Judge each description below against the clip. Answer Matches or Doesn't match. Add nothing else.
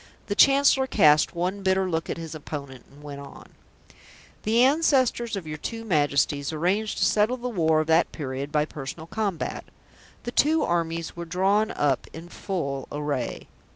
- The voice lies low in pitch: Doesn't match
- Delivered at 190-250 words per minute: Doesn't match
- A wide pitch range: Matches